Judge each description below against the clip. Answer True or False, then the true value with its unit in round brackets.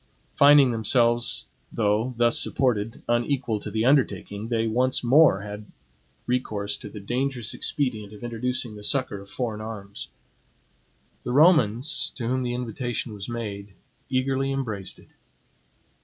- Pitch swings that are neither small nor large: True (3.4 semitones)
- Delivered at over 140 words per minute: False (135 wpm)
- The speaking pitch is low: True (120 Hz)